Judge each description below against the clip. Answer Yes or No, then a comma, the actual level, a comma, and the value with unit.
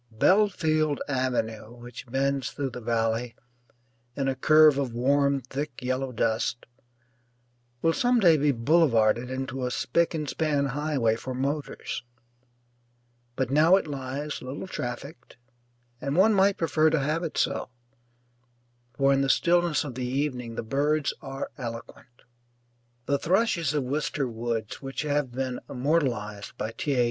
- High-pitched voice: No, low, 135 Hz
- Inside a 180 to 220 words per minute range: No, average, 145 wpm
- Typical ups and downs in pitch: Yes, average, 3.6 semitones